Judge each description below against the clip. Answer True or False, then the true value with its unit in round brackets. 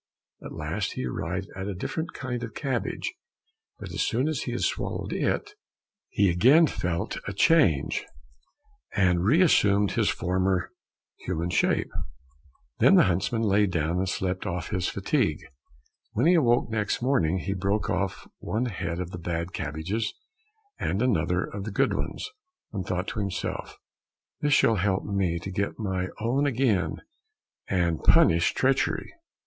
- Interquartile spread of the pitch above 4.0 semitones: True (4.4 semitones)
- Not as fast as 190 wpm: True (155 wpm)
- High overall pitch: False (100 Hz)